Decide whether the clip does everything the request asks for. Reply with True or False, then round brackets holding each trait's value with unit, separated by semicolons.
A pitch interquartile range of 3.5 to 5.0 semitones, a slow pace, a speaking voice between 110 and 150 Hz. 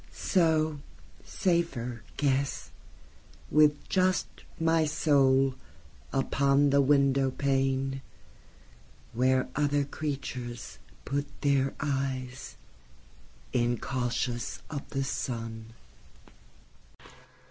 False (2.5 semitones; 60 wpm; 135 Hz)